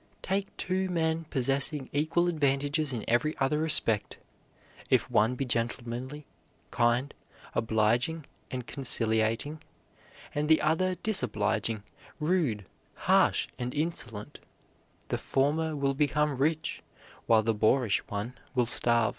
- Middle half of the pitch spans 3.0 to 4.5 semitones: No, average, 5.0 semitones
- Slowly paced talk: Yes, slow, 115 wpm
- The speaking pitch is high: No, low, 135 Hz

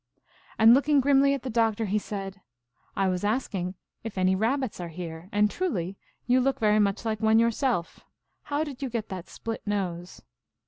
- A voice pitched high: Yes, high, 215 Hz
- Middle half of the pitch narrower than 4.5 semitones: No, average, 4.8 semitones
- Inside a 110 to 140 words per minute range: No, average, 195 wpm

